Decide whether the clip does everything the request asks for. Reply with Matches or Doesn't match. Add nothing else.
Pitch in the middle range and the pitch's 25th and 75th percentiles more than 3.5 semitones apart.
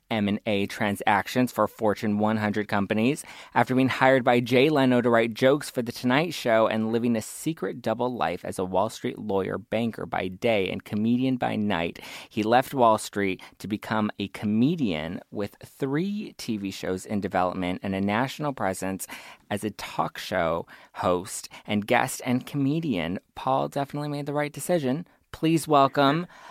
Doesn't match